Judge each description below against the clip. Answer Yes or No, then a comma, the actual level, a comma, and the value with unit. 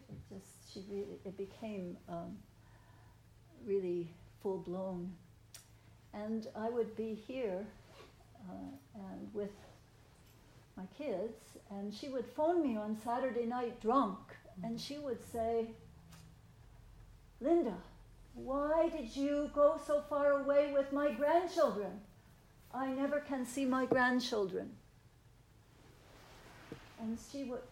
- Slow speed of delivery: Yes, slow, 115 wpm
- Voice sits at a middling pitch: No, high, 215 Hz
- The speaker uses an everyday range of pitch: No, wide, 8.3 semitones